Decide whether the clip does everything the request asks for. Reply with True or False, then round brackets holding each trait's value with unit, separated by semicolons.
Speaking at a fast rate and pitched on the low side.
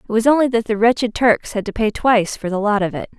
False (300 wpm; 220 Hz)